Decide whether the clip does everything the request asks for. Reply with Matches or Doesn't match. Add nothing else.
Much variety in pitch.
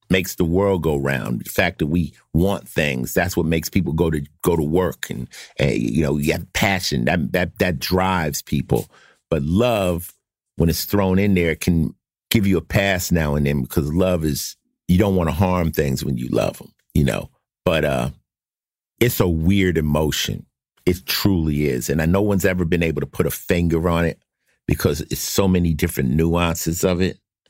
Doesn't match